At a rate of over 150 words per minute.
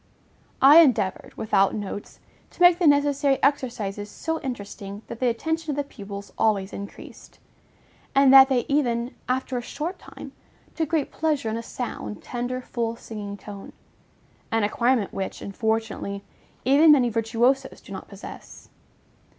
No: average, 145 wpm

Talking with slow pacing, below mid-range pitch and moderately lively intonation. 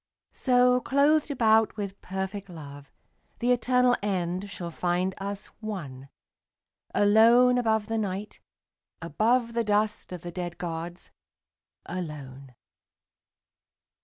No: slow, 105 wpm; high, 200 Hz; average, 4.9 semitones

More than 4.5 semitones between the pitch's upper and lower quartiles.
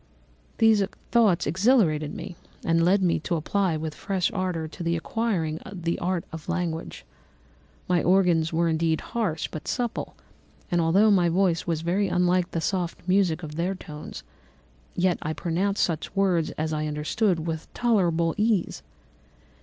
No: average, 3.1 semitones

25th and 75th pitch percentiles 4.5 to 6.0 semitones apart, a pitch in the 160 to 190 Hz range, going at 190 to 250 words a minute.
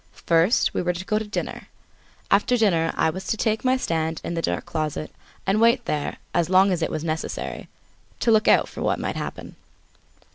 Yes: average, 4.9 semitones; medium, 185 Hz; fast, 205 wpm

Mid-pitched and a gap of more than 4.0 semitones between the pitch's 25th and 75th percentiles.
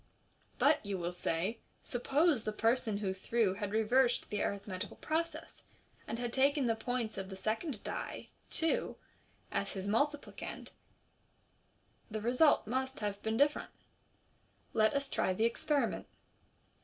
No: high, 225 Hz; average, 4.6 semitones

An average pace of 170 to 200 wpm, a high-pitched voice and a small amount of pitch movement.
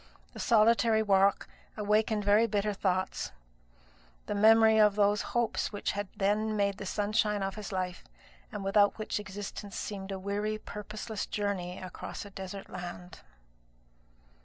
No: average, 140 wpm; high, 205 Hz; narrow, 1.6 semitones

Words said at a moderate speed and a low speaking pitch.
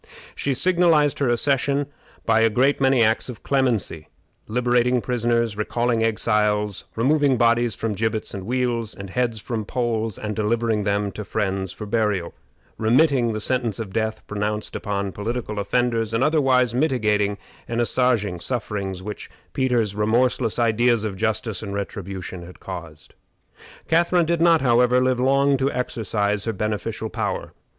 Yes: average, 145 wpm; low, 115 Hz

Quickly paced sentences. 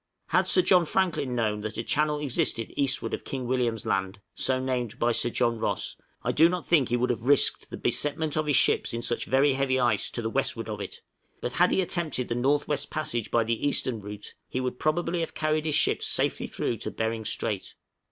Yes: fast, 220 wpm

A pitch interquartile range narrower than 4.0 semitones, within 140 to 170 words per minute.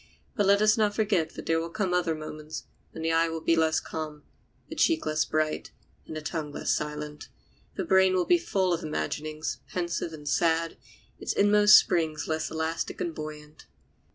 No: average, 3.3 semitones; average, 185 wpm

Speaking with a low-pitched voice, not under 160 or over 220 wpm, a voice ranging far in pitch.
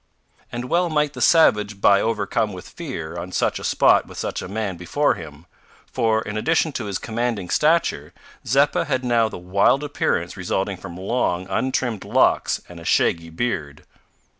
Yes: low, 105 Hz; average, 170 wpm; wide, 6.3 semitones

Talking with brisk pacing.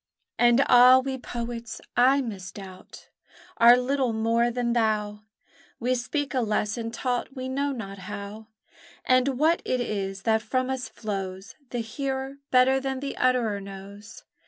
No: average, 145 wpm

